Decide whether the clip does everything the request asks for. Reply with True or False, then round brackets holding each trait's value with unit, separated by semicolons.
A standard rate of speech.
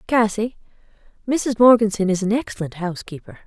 False (120 wpm)